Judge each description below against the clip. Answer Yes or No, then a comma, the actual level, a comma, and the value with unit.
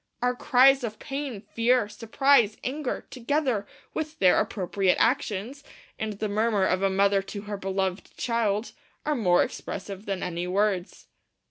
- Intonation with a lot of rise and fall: No, average, 4.3 semitones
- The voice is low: No, high, 215 Hz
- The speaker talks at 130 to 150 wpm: Yes, average, 145 wpm